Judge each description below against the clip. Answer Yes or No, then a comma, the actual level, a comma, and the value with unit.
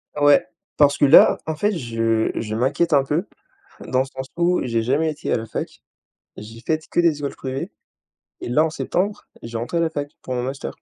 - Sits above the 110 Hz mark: Yes, medium, 140 Hz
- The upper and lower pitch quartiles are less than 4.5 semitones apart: No, average, 4.9 semitones